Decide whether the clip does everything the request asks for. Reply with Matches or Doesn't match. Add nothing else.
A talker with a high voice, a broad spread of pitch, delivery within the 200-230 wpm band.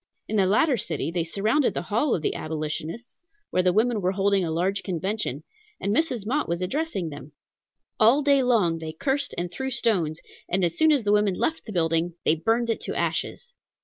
Matches